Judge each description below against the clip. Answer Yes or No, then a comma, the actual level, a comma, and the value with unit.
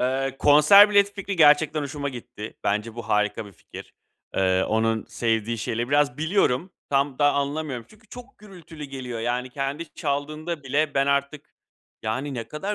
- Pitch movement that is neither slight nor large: Yes, average, 4.5 semitones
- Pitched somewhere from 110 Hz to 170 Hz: Yes, medium, 140 Hz